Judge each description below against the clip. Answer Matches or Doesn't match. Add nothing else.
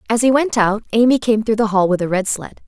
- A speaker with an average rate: Doesn't match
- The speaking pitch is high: Matches